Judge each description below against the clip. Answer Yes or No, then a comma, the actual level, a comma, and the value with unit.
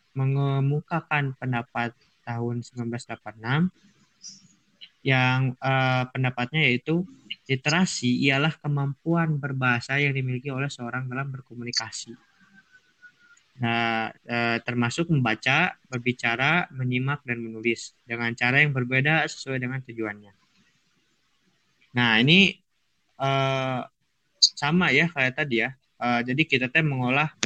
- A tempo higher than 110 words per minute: No, average, 100 wpm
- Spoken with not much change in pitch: No, average, 3.7 semitones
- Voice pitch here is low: Yes, low, 130 Hz